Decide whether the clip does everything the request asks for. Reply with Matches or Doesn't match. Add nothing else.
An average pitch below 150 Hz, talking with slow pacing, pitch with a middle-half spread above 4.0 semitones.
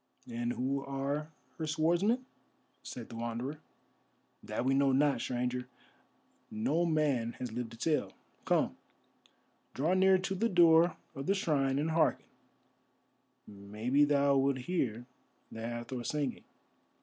Matches